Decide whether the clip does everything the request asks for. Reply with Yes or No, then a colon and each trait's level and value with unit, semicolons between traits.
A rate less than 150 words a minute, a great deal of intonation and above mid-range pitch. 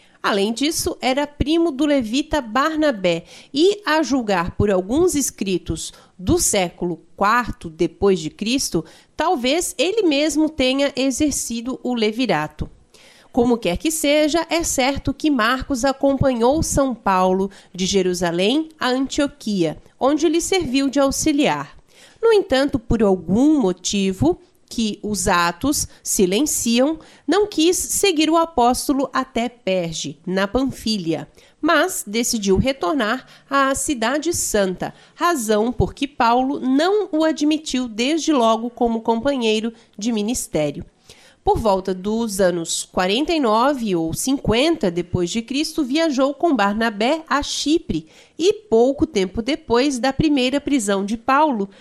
Yes: average, 125 wpm; wide, 6.7 semitones; very high, 260 Hz